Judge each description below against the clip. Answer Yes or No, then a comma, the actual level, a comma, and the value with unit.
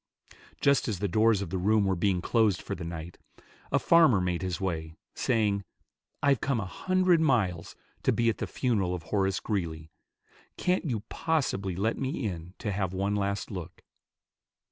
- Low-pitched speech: Yes, low, 100 Hz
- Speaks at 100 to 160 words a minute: No, average, 175 wpm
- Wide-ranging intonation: No, average, 4.3 semitones